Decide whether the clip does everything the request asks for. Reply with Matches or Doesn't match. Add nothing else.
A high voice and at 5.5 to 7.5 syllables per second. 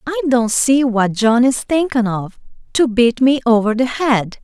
Doesn't match